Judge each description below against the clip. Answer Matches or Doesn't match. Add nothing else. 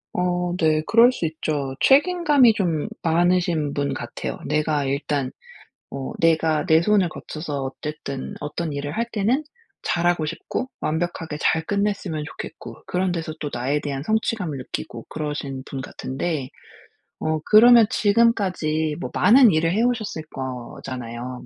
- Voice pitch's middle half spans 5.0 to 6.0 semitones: Matches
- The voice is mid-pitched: Matches